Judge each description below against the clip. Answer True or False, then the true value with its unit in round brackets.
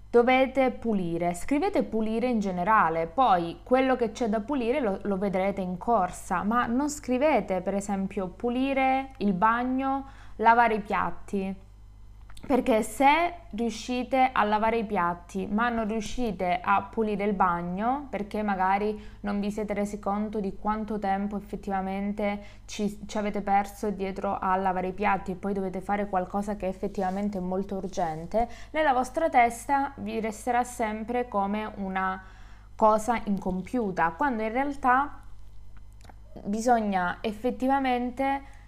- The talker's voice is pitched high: True (210 Hz)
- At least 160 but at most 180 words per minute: False (135 wpm)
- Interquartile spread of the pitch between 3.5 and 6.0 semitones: True (3.9 semitones)